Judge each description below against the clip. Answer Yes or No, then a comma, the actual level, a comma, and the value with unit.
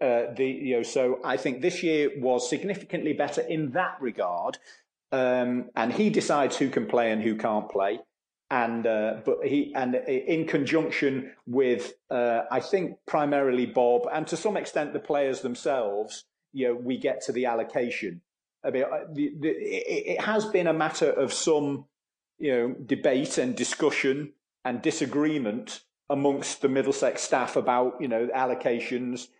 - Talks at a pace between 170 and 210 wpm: No, average, 155 wpm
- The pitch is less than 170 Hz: Yes, medium, 140 Hz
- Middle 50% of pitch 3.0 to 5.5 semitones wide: Yes, average, 4.3 semitones